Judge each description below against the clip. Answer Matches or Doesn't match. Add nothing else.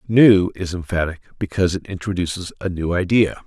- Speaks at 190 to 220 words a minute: Doesn't match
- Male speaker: Matches